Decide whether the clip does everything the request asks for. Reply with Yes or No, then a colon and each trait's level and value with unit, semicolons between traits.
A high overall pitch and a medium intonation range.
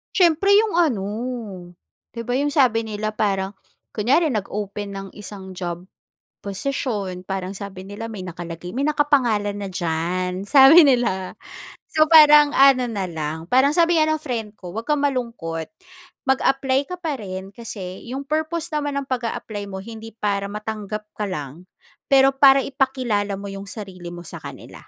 No: high, 215 Hz; wide, 6.1 semitones